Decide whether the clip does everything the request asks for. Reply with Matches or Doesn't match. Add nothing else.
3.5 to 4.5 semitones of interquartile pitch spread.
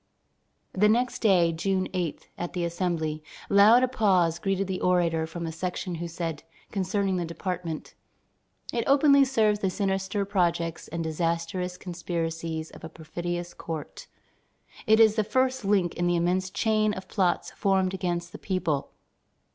Doesn't match